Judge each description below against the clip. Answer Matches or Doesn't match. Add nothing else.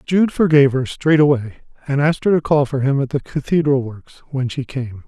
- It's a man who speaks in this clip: Matches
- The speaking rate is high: Matches